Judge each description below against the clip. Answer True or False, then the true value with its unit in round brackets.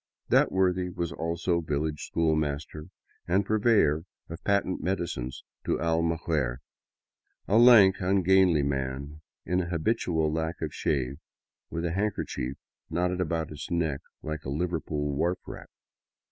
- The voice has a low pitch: True (85 Hz)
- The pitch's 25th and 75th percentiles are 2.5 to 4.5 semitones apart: True (3.2 semitones)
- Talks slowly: True (130 wpm)